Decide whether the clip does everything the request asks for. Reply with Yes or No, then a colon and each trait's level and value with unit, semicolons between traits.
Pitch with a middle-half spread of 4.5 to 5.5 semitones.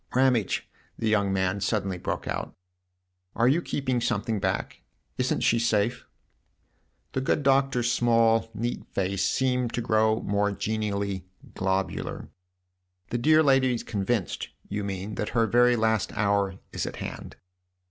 No: average, 3.5 semitones